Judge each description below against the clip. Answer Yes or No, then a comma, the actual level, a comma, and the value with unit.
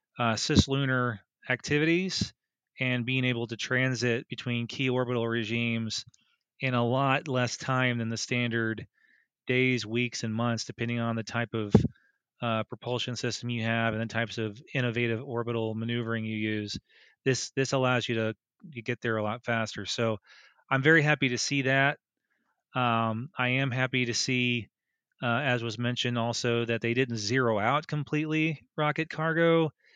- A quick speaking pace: No, average, 160 wpm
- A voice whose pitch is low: Yes, low, 120 Hz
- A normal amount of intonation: No, narrow, 2.2 semitones